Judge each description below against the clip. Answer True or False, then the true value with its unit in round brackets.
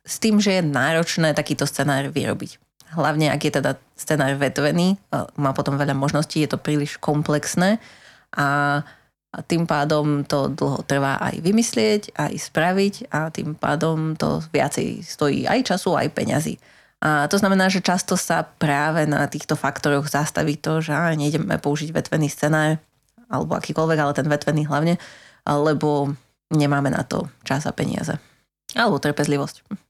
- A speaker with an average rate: True (150 wpm)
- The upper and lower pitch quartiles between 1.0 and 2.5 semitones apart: True (2.2 semitones)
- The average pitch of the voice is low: False (150 Hz)